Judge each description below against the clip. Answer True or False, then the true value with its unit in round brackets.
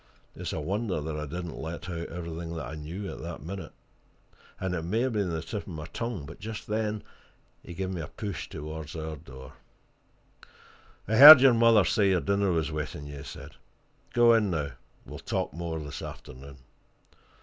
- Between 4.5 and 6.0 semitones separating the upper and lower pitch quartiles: True (5.0 semitones)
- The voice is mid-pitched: False (85 Hz)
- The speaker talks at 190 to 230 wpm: True (195 wpm)